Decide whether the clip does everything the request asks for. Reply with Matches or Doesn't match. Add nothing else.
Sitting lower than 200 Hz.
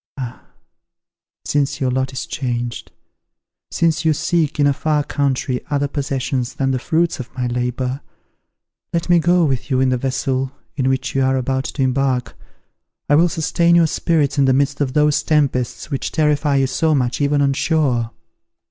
Matches